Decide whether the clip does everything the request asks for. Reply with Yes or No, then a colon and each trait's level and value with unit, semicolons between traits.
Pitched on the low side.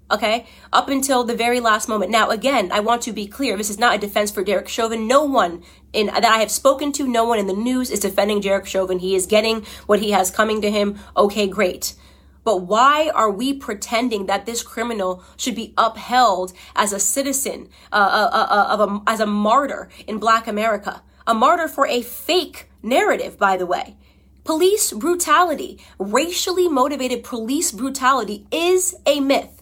No: high, 225 Hz